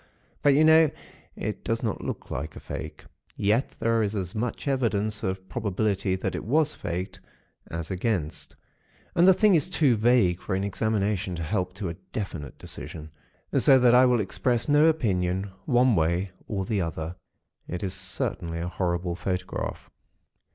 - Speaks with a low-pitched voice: Yes, low, 100 Hz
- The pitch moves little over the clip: No, average, 5.3 semitones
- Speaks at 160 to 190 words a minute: Yes, average, 165 wpm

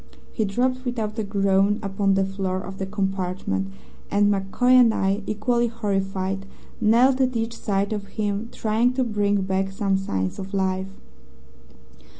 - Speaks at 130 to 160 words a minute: Yes, average, 155 wpm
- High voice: Yes, high, 200 Hz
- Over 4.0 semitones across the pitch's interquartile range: No, narrow, 2.6 semitones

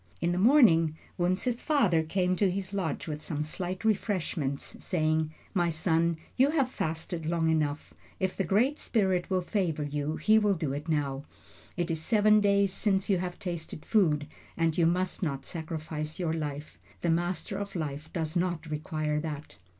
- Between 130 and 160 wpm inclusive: No, average, 175 wpm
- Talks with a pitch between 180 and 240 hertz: No, medium, 170 Hz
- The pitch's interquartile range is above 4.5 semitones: No, average, 3.6 semitones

